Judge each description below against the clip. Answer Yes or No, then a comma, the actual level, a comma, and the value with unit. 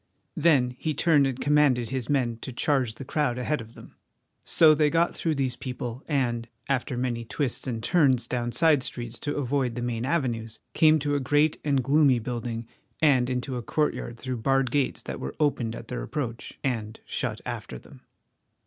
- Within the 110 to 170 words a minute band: No, average, 185 wpm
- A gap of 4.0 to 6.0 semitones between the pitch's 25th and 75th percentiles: No, average, 3.5 semitones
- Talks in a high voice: No, low, 130 Hz